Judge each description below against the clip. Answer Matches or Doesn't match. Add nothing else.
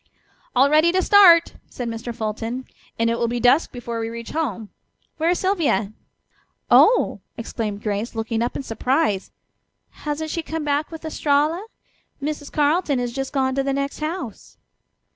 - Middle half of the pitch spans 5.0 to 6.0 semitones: Matches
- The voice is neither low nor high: Doesn't match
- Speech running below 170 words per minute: Matches